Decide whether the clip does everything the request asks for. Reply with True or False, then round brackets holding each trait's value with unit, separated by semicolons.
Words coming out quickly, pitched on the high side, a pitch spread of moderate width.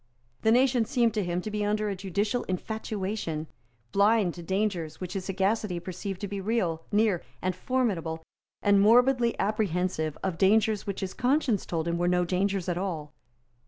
False (170 wpm; 195 Hz; 3.4 semitones)